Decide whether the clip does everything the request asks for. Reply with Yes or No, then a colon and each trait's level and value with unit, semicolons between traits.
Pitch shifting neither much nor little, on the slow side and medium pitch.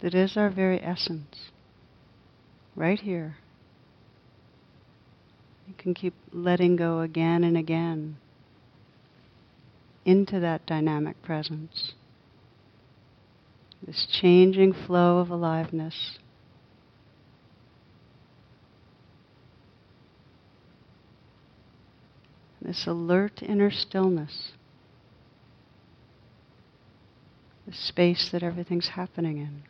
No: wide, 6.2 semitones; slow, 70 wpm; medium, 155 Hz